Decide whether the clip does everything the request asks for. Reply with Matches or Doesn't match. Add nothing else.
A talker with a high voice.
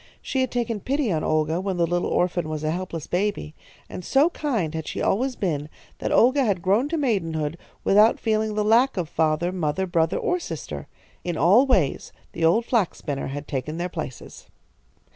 Doesn't match